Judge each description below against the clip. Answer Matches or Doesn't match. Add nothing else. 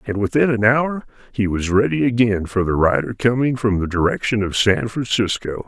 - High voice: Doesn't match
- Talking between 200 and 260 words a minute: Doesn't match